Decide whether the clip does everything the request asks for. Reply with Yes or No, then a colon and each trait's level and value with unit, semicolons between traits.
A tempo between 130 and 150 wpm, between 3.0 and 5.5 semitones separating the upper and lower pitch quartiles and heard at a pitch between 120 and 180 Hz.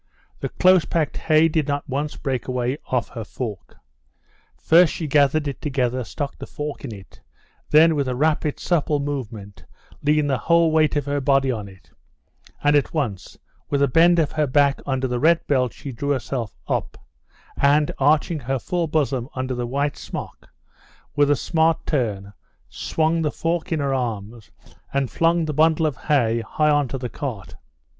No: average, 180 wpm; average, 3.4 semitones; medium, 140 Hz